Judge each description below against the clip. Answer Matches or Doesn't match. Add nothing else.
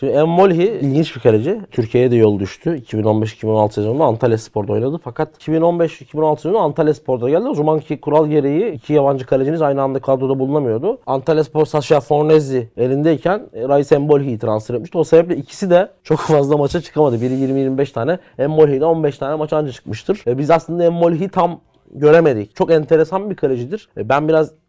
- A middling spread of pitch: Matches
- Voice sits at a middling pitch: Matches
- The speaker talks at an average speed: Doesn't match